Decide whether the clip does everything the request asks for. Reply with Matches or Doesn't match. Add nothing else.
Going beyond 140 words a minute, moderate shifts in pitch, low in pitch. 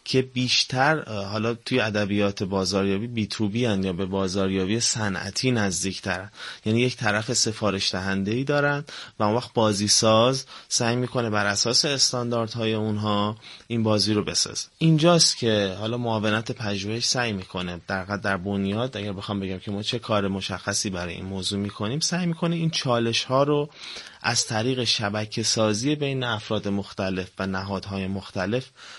Matches